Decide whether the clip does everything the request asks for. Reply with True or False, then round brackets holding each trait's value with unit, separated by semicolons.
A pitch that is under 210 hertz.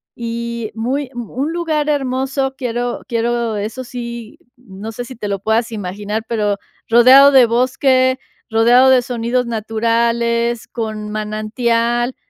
False (235 Hz)